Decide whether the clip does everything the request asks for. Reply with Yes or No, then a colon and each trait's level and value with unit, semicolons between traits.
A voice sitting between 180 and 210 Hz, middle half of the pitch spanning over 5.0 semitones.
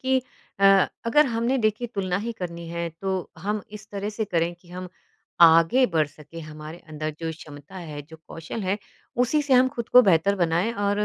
Yes: medium, 185 Hz; wide, 5.6 semitones